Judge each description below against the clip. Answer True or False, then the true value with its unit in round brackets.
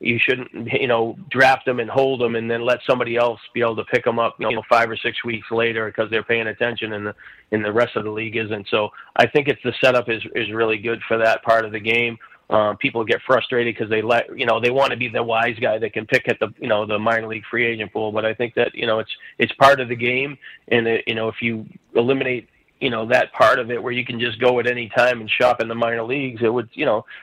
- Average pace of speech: False (280 wpm)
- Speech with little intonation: True (1.6 semitones)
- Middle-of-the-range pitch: False (115 Hz)